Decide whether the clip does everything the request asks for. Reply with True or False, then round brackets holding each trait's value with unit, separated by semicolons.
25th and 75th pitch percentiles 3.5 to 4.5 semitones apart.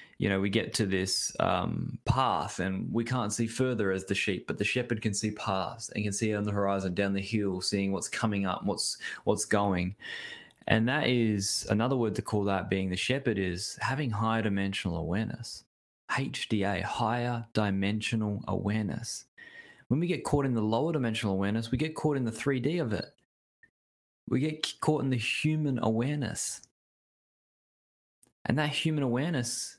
True (4.0 semitones)